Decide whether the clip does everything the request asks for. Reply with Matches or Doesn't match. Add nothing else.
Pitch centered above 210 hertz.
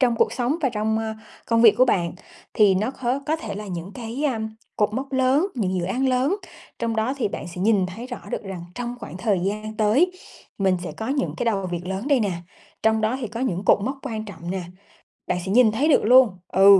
Matches